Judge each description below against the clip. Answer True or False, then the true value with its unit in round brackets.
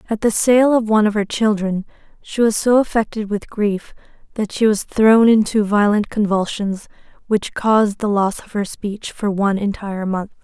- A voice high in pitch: True (210 Hz)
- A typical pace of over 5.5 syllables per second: False (4.9 syllables/s)